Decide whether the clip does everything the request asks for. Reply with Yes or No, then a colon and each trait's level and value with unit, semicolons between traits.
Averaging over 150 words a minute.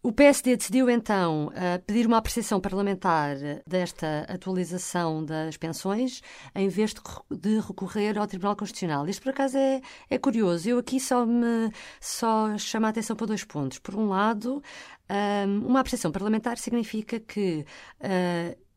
No: average, 135 wpm